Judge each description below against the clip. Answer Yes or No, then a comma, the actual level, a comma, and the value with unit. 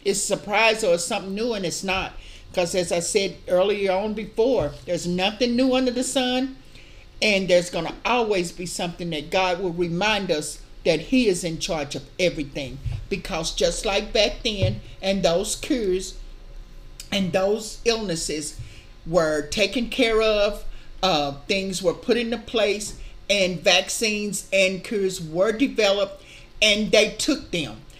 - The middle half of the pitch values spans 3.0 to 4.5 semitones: Yes, average, 3.7 semitones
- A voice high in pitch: Yes, high, 195 Hz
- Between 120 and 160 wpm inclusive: Yes, average, 155 wpm